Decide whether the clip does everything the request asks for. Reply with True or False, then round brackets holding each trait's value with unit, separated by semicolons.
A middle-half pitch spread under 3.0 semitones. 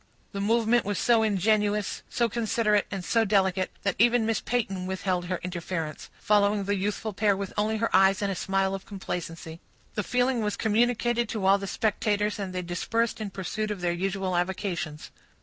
True (2.6 semitones)